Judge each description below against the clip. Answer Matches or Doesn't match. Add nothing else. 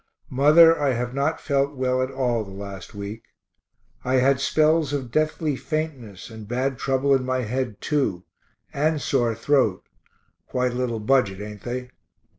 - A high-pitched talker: Doesn't match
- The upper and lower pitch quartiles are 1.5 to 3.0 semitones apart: Doesn't match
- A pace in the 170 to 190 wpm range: Doesn't match